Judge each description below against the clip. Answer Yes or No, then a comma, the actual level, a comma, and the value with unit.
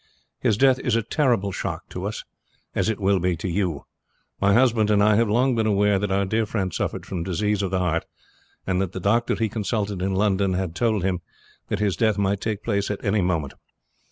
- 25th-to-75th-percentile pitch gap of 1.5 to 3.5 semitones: Yes, narrow, 2.4 semitones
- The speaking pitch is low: Yes, low, 100 Hz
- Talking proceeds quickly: Yes, fast, 220 wpm